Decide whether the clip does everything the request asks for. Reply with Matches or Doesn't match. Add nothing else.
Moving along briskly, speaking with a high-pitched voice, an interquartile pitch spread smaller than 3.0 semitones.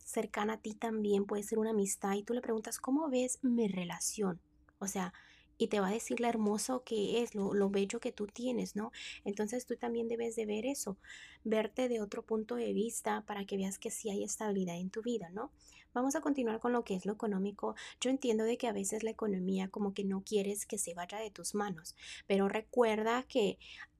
Matches